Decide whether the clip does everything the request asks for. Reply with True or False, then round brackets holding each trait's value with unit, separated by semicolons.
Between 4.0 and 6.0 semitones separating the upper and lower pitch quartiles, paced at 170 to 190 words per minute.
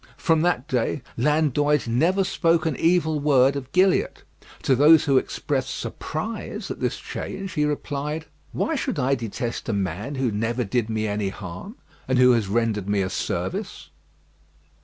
False (5.5 semitones; 160 wpm)